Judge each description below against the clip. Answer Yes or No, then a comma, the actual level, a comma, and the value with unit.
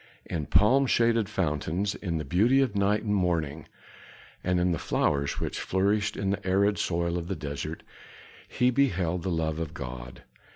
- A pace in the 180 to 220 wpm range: No, average, 170 wpm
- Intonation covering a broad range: No, average, 4.1 semitones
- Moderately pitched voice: No, very low, 90 Hz